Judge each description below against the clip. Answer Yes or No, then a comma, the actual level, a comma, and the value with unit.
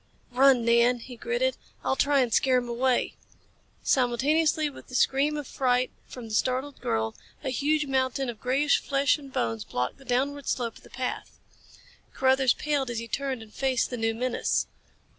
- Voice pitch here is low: No, very high, 260 Hz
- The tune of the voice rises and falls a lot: No, narrow, 2.5 semitones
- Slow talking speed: No, average, 180 wpm